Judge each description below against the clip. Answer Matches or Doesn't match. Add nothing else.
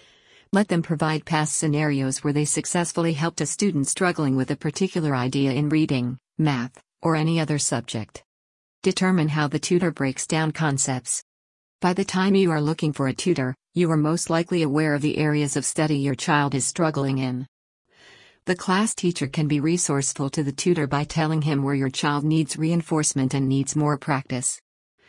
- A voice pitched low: Doesn't match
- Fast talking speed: Doesn't match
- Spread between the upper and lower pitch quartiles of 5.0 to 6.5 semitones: Doesn't match